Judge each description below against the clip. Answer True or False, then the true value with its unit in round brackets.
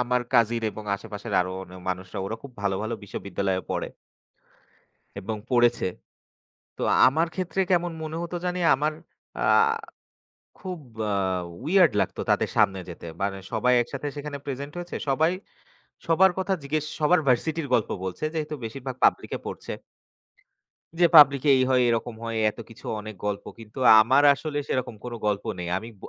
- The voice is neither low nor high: False (125 Hz)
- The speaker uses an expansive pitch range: True (6.2 semitones)